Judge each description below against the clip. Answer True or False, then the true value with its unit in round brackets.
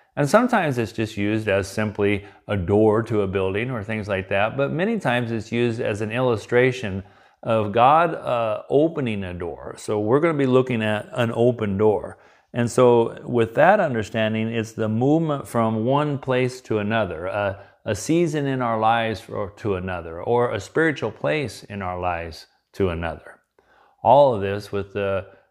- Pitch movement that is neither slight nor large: True (3.7 semitones)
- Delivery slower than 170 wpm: False (180 wpm)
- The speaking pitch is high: False (110 Hz)